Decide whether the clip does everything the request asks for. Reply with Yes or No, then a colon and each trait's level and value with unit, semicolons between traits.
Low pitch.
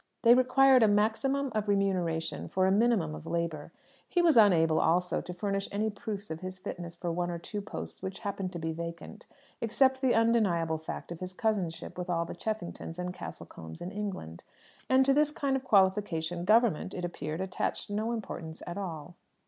No: high, 190 Hz